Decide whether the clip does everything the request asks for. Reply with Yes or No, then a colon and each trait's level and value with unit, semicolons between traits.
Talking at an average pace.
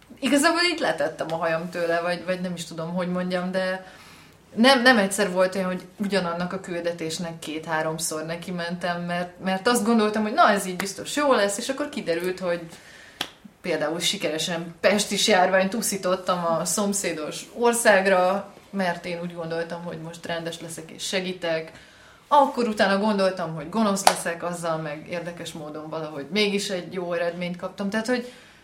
No: fast, 160 wpm